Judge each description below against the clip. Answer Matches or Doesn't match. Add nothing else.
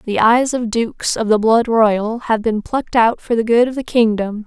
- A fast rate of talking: Matches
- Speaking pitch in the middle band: Doesn't match